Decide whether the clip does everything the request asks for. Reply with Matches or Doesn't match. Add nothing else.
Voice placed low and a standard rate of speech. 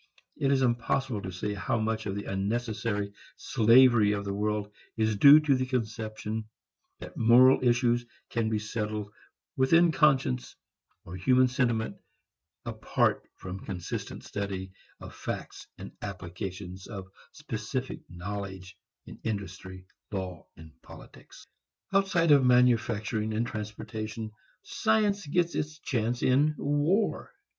Doesn't match